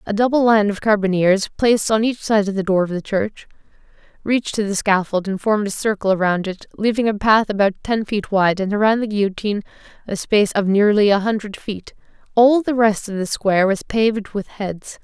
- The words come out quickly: Yes, fast, 210 wpm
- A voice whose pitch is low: No, high, 205 Hz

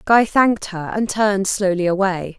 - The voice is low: No, high, 195 Hz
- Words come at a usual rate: Yes, average, 175 wpm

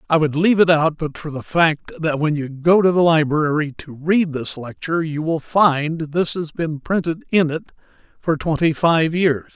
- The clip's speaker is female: No, male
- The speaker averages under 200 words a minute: No, fast, 205 wpm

